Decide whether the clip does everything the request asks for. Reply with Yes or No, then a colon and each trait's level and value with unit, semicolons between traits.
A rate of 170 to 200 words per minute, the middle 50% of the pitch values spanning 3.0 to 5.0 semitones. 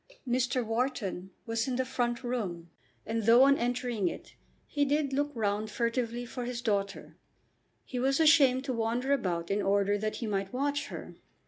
Yes: average, 175 wpm; average, 3.6 semitones